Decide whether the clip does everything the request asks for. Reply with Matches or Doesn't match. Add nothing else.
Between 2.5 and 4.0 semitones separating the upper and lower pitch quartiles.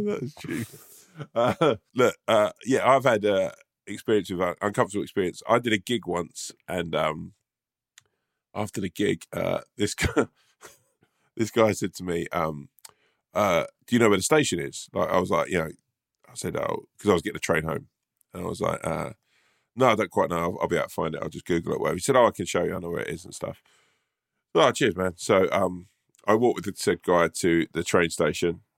Doesn't match